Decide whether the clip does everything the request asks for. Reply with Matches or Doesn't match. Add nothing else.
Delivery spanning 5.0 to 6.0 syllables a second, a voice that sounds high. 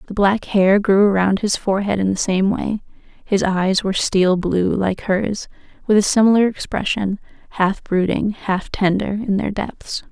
Doesn't match